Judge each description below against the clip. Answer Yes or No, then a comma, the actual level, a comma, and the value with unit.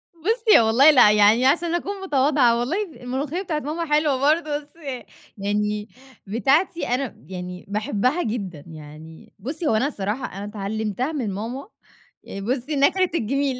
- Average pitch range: No, wide, 6.4 semitones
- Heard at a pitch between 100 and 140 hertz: No, very high, 255 Hz